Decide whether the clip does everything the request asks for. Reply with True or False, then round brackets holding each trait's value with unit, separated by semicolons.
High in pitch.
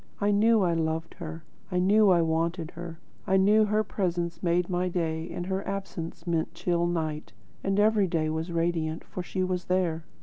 False (175 Hz)